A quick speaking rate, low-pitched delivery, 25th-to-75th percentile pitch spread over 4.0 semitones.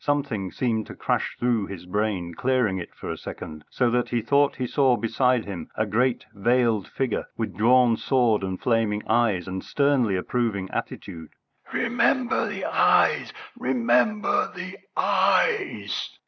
No: average, 145 wpm; low, 115 Hz; average, 4.4 semitones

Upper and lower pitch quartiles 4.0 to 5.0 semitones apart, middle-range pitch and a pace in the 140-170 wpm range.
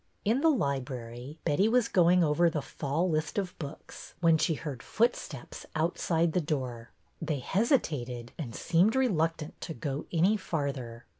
Yes: average, 4.6 semitones; medium, 160 Hz; average, 150 wpm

